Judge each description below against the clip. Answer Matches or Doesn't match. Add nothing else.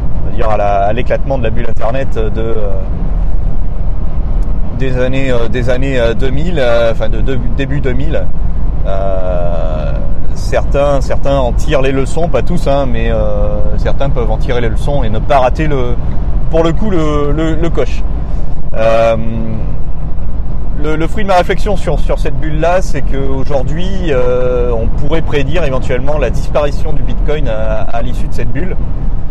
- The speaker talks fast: Doesn't match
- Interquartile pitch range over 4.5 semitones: Matches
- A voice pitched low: Matches